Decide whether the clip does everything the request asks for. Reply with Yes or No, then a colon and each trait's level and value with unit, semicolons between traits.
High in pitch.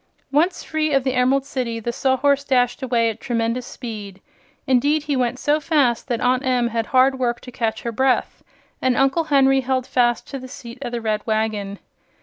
Yes: very high, 255 Hz